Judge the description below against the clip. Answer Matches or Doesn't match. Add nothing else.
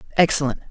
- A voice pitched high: Doesn't match